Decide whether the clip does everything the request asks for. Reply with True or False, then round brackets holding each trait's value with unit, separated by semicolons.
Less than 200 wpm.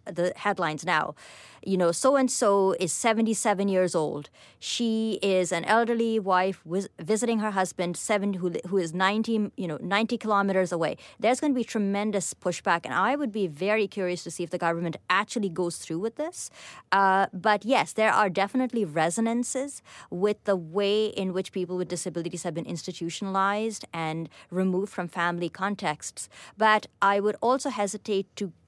True (170 wpm)